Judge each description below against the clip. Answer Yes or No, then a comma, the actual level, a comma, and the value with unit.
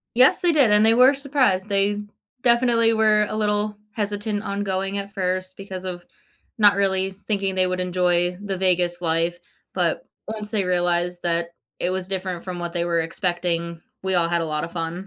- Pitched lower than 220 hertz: Yes, high, 190 Hz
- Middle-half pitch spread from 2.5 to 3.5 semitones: Yes, average, 2.9 semitones